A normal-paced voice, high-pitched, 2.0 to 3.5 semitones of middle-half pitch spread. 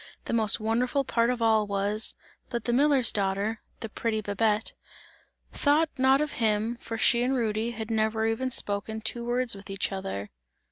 Yes: average, 175 wpm; high, 225 Hz; narrow, 2.5 semitones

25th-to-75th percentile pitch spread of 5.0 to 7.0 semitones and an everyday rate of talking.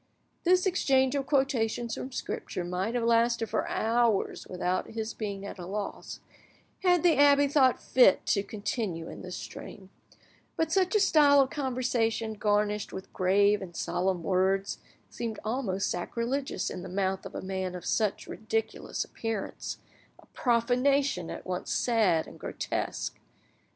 Yes: wide, 5.5 semitones; average, 145 wpm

